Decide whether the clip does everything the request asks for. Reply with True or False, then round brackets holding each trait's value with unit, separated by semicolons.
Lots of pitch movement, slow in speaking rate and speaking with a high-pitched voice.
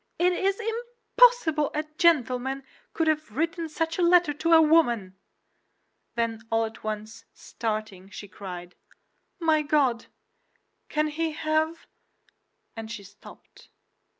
True (6.6 semitones; 125 wpm; 300 Hz)